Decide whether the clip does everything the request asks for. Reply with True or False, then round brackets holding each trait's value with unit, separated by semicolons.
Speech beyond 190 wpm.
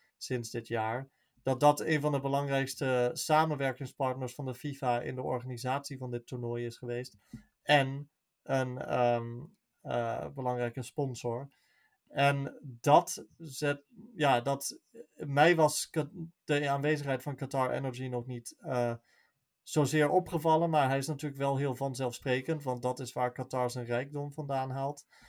False (140 wpm)